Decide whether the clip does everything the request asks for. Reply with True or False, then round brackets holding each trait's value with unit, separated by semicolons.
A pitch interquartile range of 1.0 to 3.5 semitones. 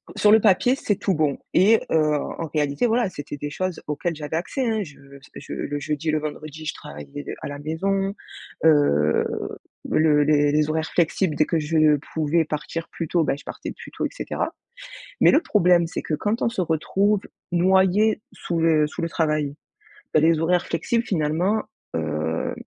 False (3.9 semitones)